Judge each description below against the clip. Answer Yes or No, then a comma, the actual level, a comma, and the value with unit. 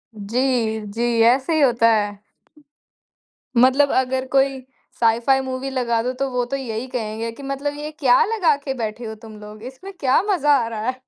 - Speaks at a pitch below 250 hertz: No, very high, 255 Hz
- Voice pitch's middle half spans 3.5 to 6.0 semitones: No, average, 3.0 semitones